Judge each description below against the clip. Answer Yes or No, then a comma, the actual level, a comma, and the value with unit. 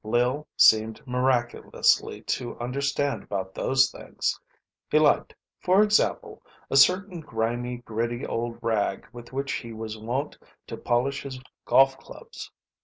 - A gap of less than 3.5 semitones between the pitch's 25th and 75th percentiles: Yes, average, 3.0 semitones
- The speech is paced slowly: Yes, slow, 130 wpm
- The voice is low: Yes, low, 125 Hz